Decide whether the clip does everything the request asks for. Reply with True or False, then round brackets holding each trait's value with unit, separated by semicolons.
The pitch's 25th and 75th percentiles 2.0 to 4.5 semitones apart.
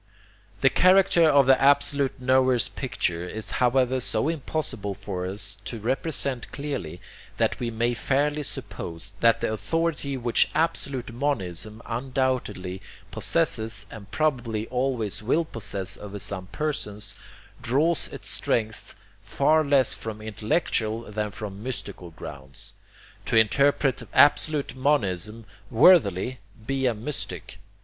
False (5.0 semitones)